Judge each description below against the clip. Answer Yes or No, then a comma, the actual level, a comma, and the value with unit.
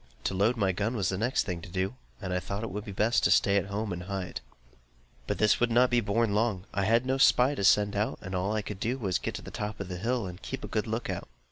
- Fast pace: Yes, fast, 300 wpm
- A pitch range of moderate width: Yes, average, 3.3 semitones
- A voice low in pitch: Yes, low, 100 Hz